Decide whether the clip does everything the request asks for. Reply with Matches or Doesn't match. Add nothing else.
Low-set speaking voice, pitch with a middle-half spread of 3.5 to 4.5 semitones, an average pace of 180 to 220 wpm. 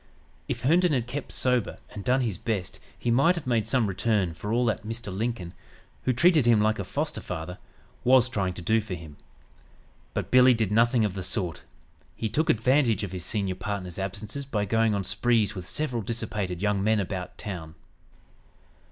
Matches